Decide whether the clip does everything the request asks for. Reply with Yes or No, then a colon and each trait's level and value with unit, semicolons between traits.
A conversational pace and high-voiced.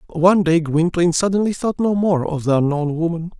No: average, 195 wpm; medium, 170 Hz